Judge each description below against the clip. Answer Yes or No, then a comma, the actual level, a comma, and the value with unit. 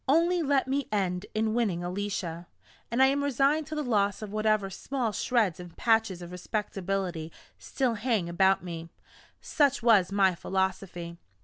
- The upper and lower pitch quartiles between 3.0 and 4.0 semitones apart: No, wide, 5.5 semitones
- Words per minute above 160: No, average, 155 wpm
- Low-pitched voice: No, high, 205 Hz